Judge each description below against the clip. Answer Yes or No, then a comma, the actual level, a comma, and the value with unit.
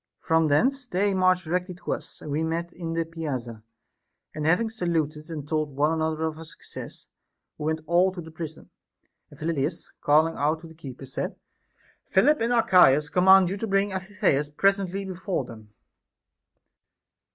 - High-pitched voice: No, medium, 165 Hz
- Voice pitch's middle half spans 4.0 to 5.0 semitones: No, average, 3.5 semitones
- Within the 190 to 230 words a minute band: No, average, 165 wpm